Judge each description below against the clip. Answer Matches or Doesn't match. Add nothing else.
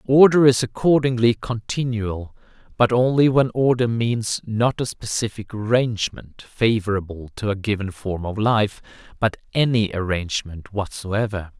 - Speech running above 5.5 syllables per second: Doesn't match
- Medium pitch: Doesn't match